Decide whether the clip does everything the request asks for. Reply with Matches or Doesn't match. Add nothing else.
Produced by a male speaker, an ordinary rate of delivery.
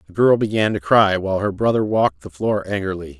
Doesn't match